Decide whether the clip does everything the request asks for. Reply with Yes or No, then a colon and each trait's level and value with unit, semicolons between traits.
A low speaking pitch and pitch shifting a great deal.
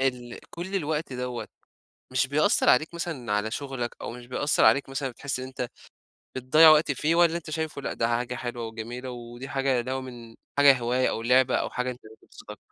No: low, 130 Hz; average, 2.9 semitones